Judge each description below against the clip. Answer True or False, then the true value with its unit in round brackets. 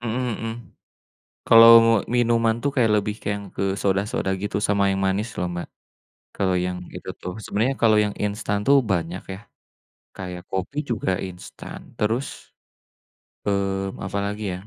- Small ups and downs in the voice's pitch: False (3.0 semitones)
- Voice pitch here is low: True (100 Hz)